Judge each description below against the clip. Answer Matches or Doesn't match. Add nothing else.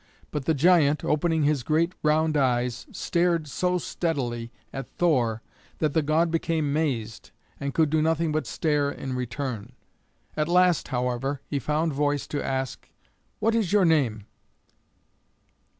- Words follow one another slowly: Doesn't match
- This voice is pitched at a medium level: Matches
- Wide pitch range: Doesn't match